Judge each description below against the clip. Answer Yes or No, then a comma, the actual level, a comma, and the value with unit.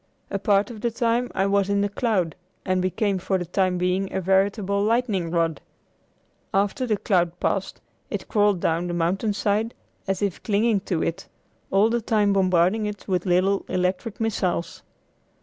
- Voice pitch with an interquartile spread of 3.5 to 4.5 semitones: No, narrow, 2.5 semitones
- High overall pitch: Yes, high, 195 Hz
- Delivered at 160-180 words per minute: Yes, average, 165 wpm